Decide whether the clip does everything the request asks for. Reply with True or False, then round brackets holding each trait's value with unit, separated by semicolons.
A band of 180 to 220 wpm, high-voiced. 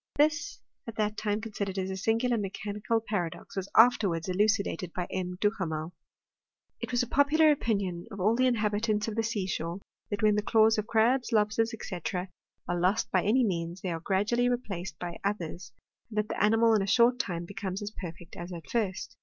True (195 wpm; 210 Hz)